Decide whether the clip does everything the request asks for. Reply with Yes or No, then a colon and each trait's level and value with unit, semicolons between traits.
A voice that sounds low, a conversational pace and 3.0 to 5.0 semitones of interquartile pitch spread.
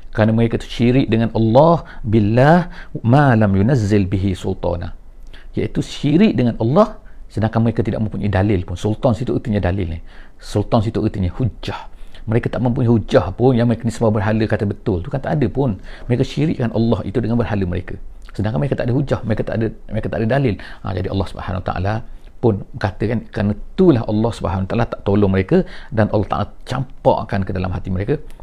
Yes: low, 110 Hz; average, 190 wpm; average, 3.5 semitones